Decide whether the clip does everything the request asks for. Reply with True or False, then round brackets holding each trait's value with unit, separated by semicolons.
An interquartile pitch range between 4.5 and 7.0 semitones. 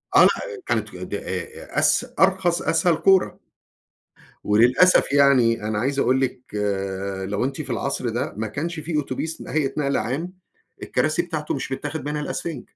True (4.8 semitones)